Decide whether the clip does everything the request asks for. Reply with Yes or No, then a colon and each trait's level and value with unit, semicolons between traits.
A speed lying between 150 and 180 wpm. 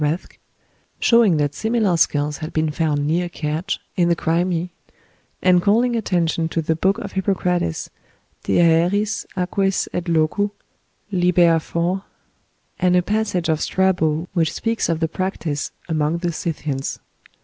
No: average, 140 wpm